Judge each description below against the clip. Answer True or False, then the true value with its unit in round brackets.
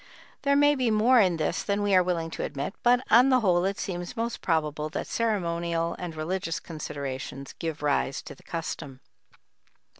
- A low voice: False (175 Hz)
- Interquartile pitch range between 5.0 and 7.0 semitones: True (5.5 semitones)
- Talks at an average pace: True (180 wpm)